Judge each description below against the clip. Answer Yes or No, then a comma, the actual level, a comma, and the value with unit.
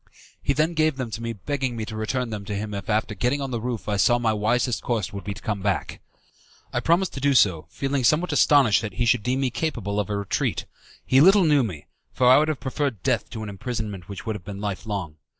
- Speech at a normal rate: No, fast, 255 wpm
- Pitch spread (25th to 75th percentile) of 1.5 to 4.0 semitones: No, average, 4.5 semitones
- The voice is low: Yes, low, 115 Hz